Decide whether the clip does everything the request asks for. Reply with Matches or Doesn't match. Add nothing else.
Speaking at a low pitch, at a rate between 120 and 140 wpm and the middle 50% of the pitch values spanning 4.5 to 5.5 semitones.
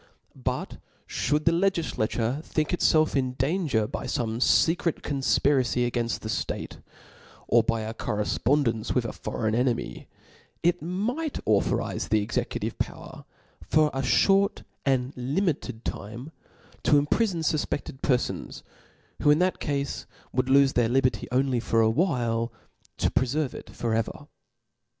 Matches